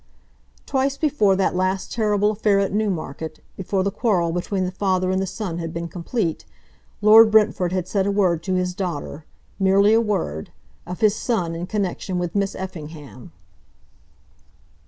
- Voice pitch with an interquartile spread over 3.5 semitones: No, average, 3.1 semitones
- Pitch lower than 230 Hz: Yes, high, 190 Hz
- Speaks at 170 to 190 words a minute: No, average, 160 wpm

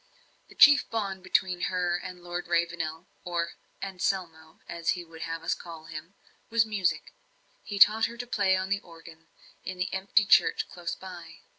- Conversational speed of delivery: Yes, average, 170 wpm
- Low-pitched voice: No, medium, 180 Hz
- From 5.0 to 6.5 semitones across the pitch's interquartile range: No, average, 2.7 semitones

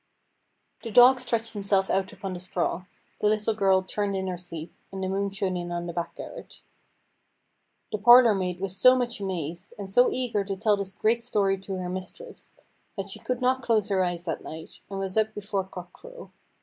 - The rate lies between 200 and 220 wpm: Yes, fast, 205 wpm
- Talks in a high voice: Yes, high, 195 Hz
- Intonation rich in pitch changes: No, average, 2.9 semitones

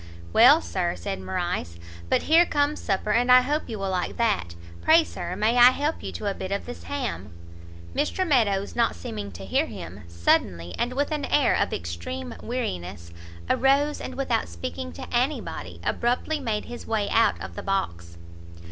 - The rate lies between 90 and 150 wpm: No, average, 180 wpm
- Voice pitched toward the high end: Yes, high, 210 Hz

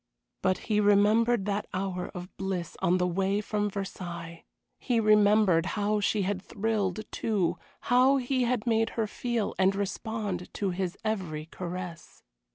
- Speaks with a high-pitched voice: Yes, high, 200 Hz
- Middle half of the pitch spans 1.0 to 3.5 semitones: Yes, average, 3.0 semitones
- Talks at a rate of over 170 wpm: No, average, 150 wpm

